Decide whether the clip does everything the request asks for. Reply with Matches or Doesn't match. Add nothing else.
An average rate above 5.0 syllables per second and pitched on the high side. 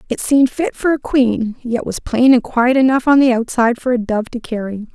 Matches